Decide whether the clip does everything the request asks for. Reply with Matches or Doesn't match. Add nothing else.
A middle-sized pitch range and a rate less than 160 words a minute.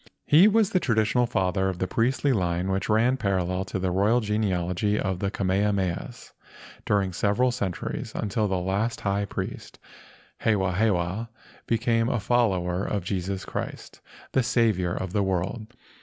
Matches